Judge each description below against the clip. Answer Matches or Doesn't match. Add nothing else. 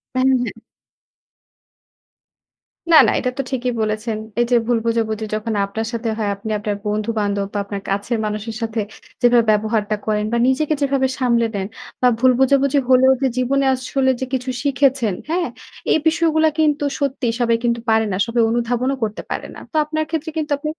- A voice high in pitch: Matches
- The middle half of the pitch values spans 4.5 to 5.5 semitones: Doesn't match